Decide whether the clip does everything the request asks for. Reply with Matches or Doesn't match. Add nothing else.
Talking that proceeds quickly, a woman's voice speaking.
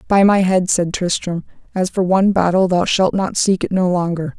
Matches